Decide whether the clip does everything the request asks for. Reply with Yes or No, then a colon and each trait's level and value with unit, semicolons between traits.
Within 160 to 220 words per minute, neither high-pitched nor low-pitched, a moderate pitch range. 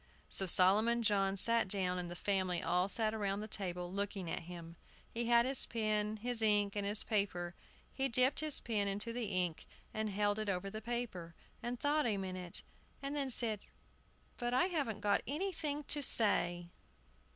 No: average, 180 wpm; high, 210 Hz; average, 4.1 semitones